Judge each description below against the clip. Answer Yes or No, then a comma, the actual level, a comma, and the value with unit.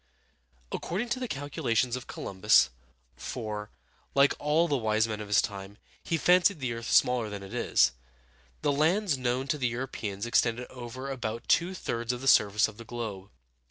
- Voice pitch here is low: Yes, low, 120 Hz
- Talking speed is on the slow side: No, average, 175 wpm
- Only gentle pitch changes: No, average, 4.7 semitones